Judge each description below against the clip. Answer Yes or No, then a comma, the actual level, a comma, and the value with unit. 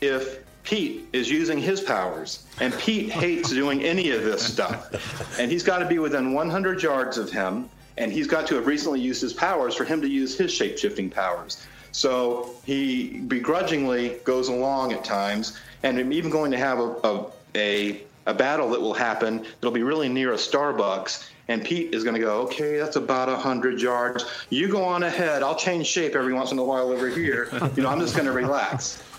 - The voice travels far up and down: Yes, wide, 5.7 semitones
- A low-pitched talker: Yes, low, 130 Hz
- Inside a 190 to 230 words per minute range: Yes, fast, 205 wpm